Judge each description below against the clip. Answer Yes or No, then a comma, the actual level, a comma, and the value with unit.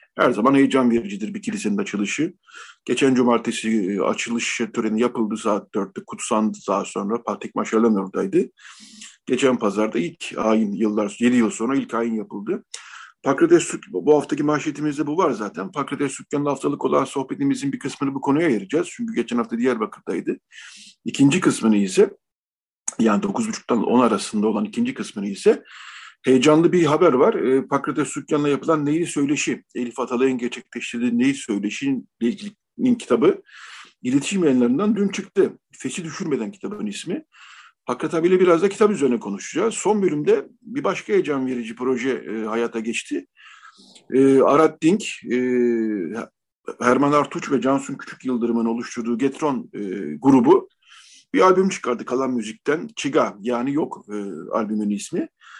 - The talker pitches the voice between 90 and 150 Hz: Yes, medium, 140 Hz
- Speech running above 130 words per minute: Yes, fast, 140 wpm